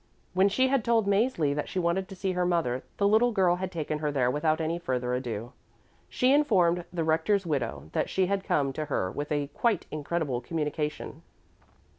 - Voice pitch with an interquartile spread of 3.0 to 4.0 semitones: No, average, 4.8 semitones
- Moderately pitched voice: Yes, medium, 170 Hz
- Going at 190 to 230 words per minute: Yes, average, 195 wpm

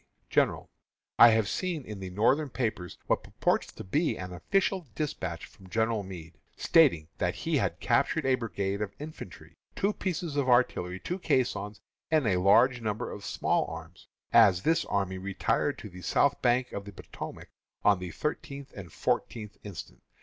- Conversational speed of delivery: Yes, average, 170 wpm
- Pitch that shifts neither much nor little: No, wide, 6.8 semitones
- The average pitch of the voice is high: No, low, 105 Hz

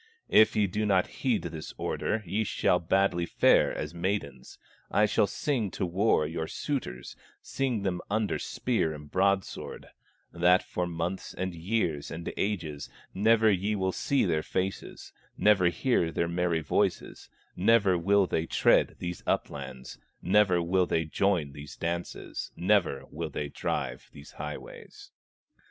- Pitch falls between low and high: No, very low, 90 Hz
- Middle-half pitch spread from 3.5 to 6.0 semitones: Yes, average, 3.9 semitones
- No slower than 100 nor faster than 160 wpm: Yes, average, 145 wpm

